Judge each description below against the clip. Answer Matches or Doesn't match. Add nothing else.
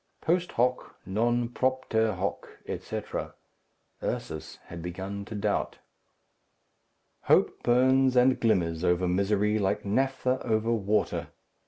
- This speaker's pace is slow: Matches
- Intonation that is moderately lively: Matches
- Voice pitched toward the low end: Matches